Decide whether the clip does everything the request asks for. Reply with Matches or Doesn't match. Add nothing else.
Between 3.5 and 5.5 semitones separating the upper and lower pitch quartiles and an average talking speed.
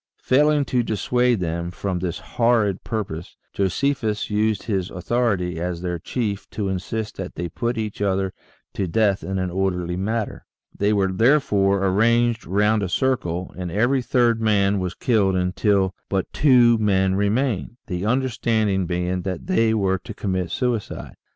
Matches